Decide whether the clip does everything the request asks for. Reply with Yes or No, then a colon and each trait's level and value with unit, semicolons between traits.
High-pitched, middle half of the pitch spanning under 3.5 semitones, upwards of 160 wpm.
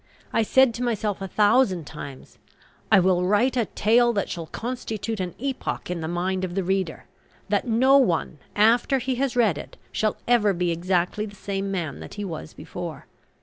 No: high, 200 Hz; average, 4.8 semitones; average, 190 wpm